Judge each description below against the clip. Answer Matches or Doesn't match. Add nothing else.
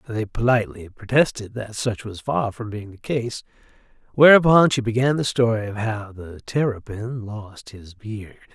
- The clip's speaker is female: Doesn't match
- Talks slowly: Doesn't match